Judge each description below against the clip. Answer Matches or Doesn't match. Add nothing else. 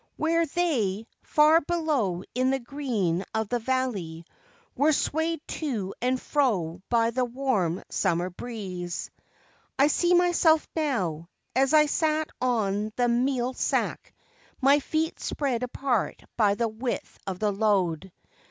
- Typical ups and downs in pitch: Doesn't match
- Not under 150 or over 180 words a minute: Doesn't match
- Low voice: Doesn't match